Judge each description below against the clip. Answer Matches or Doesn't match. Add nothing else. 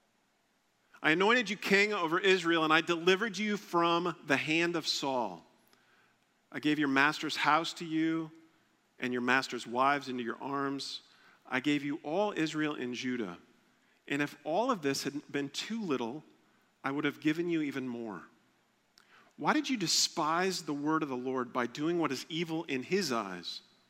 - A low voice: Doesn't match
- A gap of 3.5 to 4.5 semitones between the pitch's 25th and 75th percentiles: Matches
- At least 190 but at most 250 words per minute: Doesn't match